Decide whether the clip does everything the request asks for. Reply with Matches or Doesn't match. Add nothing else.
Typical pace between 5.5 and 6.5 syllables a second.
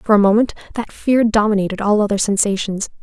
Matches